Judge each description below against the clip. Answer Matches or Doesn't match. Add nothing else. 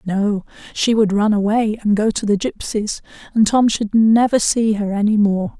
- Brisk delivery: Doesn't match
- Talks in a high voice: Matches